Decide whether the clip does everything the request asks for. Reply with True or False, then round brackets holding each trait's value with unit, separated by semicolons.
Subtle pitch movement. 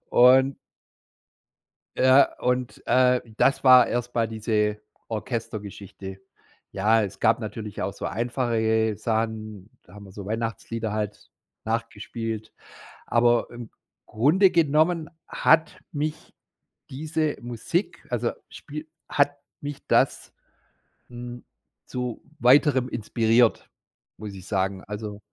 False (3.0 semitones)